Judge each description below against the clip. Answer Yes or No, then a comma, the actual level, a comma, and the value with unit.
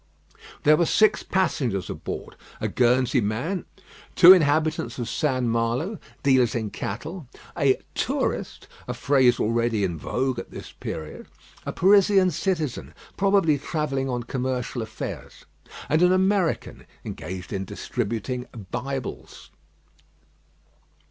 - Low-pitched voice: Yes, low, 130 Hz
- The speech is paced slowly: Yes, slow, 115 wpm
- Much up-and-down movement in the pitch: Yes, wide, 5.9 semitones